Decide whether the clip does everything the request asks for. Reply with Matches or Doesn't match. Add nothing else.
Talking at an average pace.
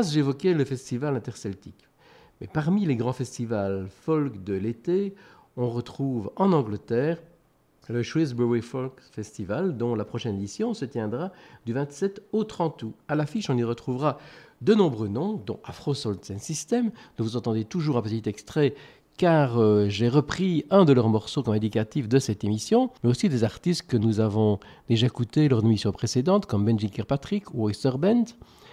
Matches